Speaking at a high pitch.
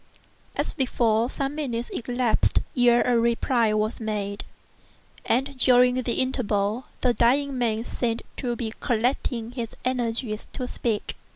Yes: high, 240 Hz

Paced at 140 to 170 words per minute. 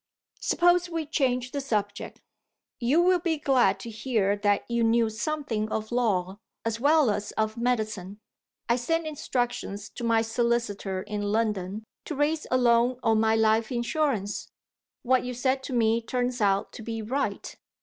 Yes: average, 160 wpm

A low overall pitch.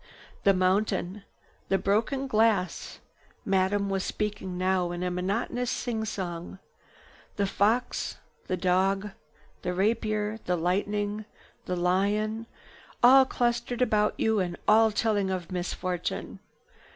No: high, 200 Hz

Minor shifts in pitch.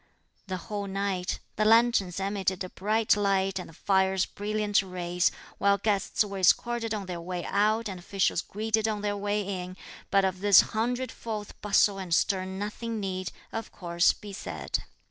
Yes: narrow, 2.2 semitones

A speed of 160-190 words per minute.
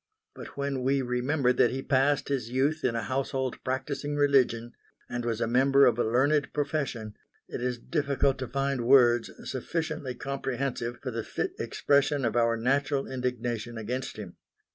Yes: average, 165 wpm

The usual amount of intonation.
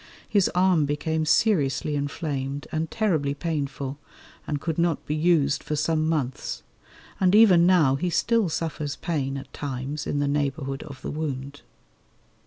Yes: average, 3.0 semitones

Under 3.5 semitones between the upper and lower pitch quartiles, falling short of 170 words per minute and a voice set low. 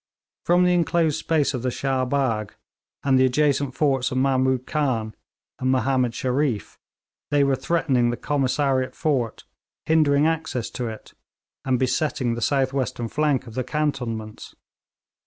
Yes: narrow, 2.6 semitones; average, 145 wpm; low, 130 Hz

